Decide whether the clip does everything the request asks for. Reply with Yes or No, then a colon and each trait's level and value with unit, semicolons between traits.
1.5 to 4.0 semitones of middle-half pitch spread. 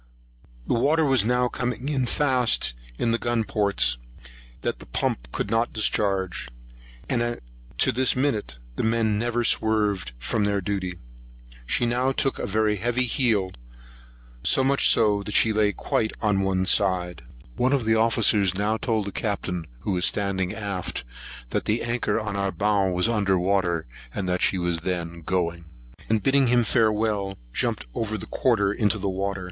Yes: average, 3.7 semitones